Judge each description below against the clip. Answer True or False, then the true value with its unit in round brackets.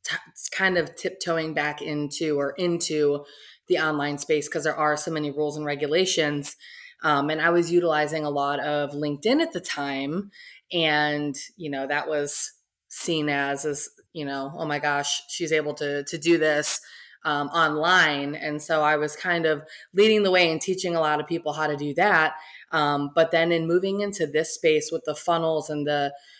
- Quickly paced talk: False (190 wpm)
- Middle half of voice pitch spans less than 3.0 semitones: True (2.4 semitones)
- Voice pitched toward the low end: False (155 Hz)